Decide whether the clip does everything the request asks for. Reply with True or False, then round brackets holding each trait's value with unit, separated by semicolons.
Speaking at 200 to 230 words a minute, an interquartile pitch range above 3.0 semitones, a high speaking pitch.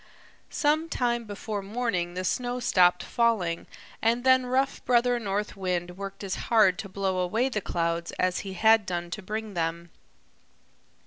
False (155 wpm; 4.7 semitones; 200 Hz)